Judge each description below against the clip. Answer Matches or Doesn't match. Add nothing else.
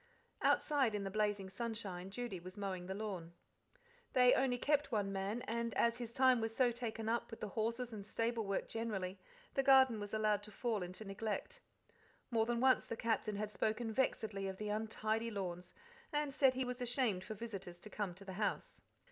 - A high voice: Matches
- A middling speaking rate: Matches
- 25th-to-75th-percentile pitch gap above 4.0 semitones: Doesn't match